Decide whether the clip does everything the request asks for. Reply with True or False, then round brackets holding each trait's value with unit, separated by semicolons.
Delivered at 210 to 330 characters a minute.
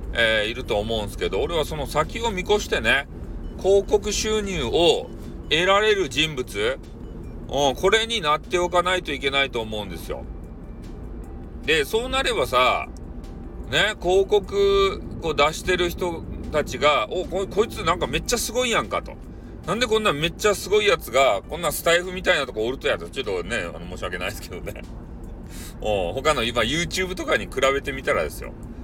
False (350 characters per minute)